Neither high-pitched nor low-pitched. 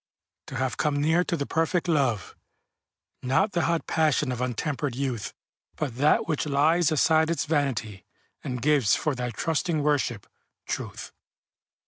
Yes: medium, 145 Hz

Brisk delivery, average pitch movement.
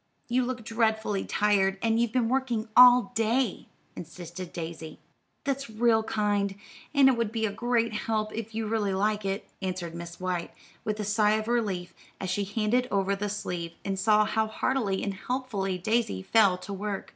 No: average, 180 wpm; average, 3.0 semitones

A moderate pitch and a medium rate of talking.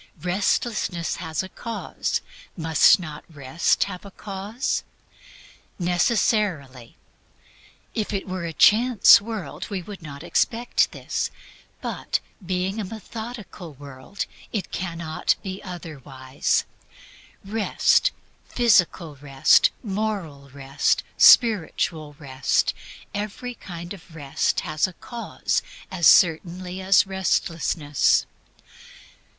No: medium, 180 Hz; slow, 100 wpm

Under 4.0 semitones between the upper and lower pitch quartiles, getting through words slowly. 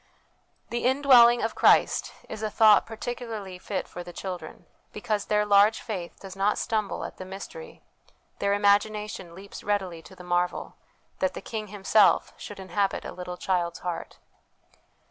No: average, 2.8 semitones; average, 155 wpm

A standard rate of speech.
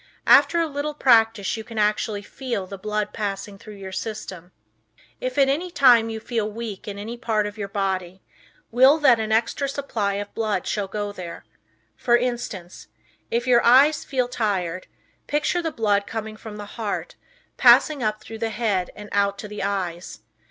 Yes: average, 180 wpm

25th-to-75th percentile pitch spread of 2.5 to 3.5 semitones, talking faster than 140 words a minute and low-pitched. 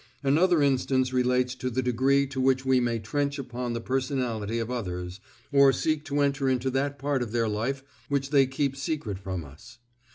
Yes: average, 2.8 semitones; average, 190 wpm; low, 130 Hz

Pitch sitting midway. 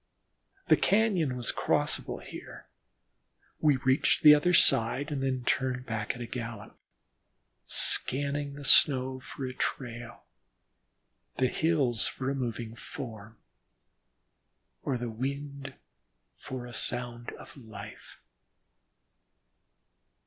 No: low, 130 Hz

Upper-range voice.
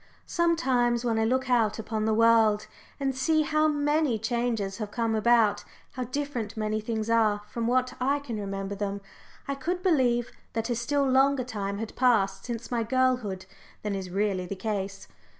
Yes: high, 230 Hz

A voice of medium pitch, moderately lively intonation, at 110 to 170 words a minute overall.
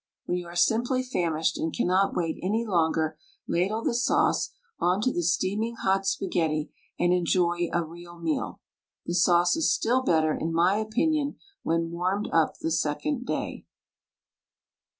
Yes: medium, 175 Hz; average, 4.3 semitones; average, 150 wpm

